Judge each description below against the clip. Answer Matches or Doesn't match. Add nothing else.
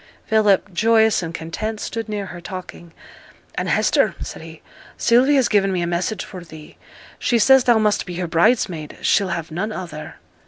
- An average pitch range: Matches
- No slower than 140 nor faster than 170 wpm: Doesn't match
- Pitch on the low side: Doesn't match